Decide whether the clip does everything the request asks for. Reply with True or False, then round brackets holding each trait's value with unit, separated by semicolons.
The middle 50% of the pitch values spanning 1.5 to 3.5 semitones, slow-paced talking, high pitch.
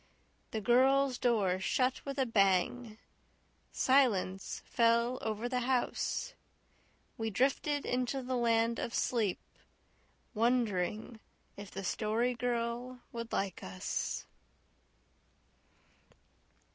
True (2.9 semitones; 95 wpm; 235 Hz)